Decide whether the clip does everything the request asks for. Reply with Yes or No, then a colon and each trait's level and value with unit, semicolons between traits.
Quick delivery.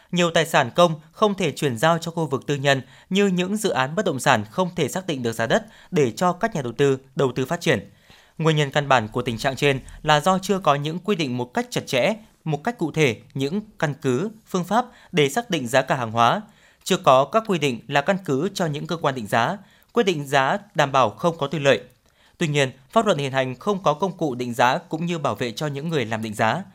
Yes: fast, 260 wpm